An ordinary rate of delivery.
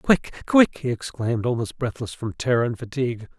Yes: average, 175 wpm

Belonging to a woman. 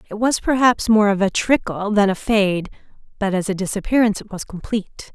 Yes: female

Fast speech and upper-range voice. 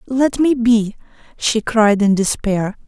No: average, 145 wpm; high, 225 Hz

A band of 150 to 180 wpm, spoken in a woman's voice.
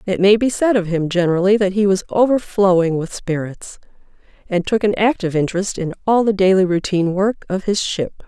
No: average, 195 wpm; female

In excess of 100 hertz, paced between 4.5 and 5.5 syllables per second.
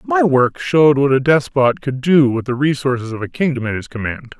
Yes: low, 135 Hz; 5.4 syllables/s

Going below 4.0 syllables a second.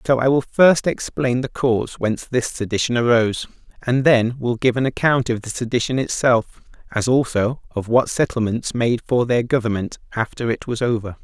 No: 5.1 syllables/s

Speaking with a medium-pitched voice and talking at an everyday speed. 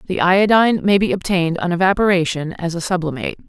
Yes: medium, 180 Hz; average, 170 wpm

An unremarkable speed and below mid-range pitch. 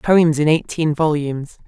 No: average, 145 wpm; medium, 155 Hz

